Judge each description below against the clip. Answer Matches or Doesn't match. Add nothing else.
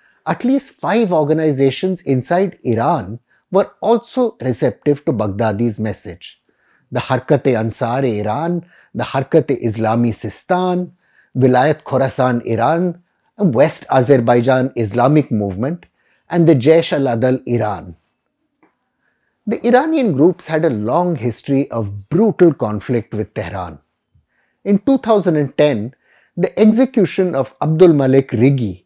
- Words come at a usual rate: Doesn't match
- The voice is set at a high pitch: Doesn't match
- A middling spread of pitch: Doesn't match